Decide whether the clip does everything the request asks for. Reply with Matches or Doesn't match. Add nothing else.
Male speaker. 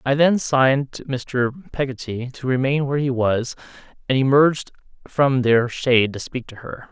Matches